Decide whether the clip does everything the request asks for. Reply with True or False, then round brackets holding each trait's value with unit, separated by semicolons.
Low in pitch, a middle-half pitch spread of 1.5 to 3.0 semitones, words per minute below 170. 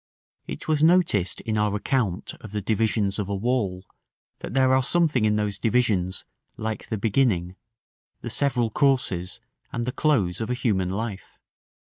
False (110 Hz; 4.4 semitones; 160 wpm)